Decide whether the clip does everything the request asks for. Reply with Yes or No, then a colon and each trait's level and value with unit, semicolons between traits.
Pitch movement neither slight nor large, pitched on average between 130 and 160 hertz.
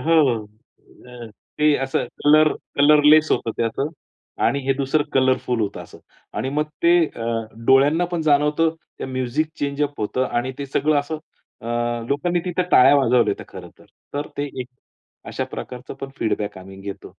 Yes: average, 3.9 semitones; low, 135 Hz